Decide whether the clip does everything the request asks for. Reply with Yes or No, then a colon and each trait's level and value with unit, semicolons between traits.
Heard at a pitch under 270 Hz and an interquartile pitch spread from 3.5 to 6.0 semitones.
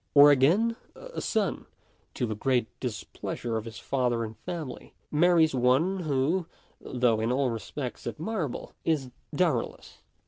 Yes: low, 135 Hz; wide, 5.6 semitones